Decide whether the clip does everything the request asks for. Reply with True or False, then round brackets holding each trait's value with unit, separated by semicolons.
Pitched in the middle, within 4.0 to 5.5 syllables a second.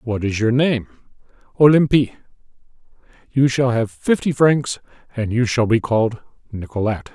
False (120 Hz; 5.0 syllables/s)